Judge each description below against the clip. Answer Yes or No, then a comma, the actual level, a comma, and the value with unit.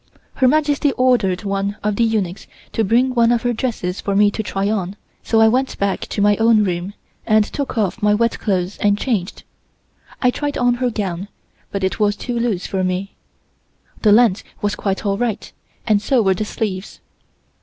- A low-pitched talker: No, high, 210 Hz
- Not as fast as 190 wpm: No, average, 195 wpm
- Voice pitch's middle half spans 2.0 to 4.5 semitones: Yes, average, 3.2 semitones